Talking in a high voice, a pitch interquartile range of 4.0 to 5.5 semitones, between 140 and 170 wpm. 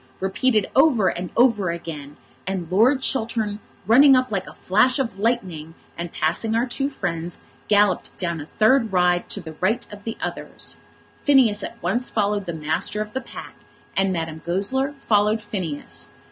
Yes: high, 205 Hz; average, 5.1 semitones; average, 165 wpm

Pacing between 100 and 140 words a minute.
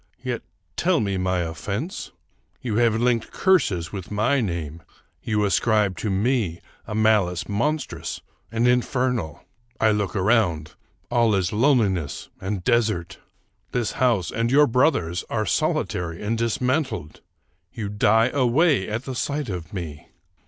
Yes: slow, 135 wpm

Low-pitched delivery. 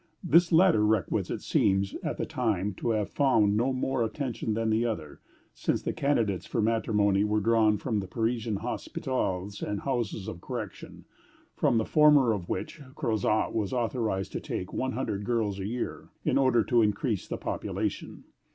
Yes: low, 110 Hz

